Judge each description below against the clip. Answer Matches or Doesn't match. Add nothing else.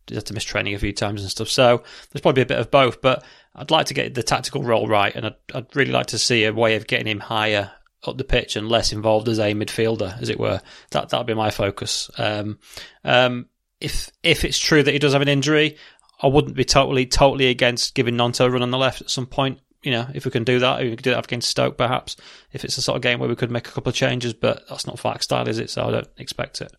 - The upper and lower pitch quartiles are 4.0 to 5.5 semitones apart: Doesn't match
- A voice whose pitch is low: Matches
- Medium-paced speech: Doesn't match